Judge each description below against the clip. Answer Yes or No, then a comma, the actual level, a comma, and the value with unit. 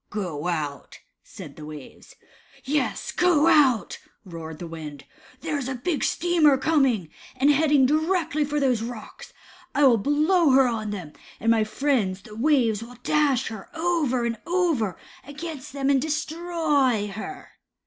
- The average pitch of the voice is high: Yes, very high, 265 Hz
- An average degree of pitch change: No, wide, 5.9 semitones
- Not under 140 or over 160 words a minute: Yes, average, 150 wpm